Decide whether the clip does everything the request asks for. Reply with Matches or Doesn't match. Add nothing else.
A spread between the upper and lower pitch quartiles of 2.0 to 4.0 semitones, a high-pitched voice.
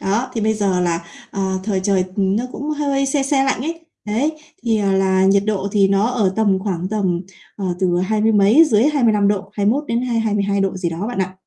Matches